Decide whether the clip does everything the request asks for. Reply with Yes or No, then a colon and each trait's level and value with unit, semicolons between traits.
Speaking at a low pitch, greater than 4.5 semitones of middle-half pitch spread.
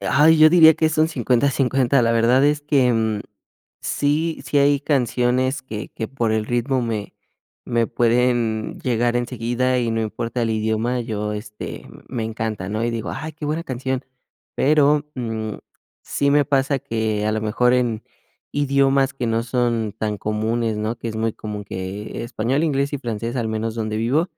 No: low, 120 Hz; average, 3.7 semitones